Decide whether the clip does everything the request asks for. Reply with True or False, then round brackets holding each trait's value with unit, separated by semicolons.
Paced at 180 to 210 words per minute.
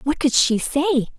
True (205 wpm)